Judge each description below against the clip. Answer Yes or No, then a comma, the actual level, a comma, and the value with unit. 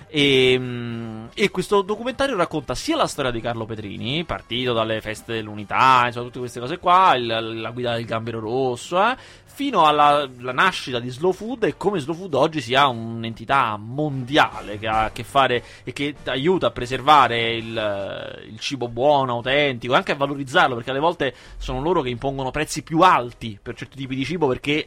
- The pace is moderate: No, fast, 185 wpm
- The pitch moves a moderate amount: Yes, average, 4.7 semitones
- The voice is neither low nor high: No, low, 130 Hz